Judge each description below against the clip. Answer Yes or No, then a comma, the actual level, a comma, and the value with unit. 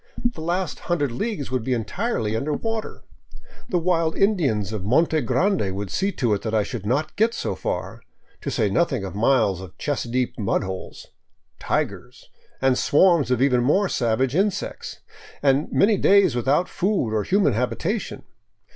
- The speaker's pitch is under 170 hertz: Yes, low, 135 Hz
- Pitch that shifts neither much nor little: No, wide, 8.4 semitones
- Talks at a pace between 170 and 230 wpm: Yes, average, 175 wpm